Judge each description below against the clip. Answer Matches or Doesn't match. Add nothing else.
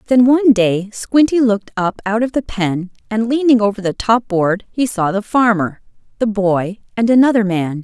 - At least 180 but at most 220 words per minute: Matches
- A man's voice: Doesn't match